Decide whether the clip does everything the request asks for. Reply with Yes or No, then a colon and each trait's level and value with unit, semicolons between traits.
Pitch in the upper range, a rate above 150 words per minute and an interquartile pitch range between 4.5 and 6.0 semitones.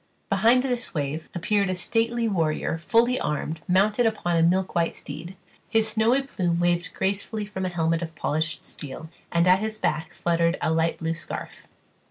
No: medium, 175 Hz; average, 175 wpm; average, 4.8 semitones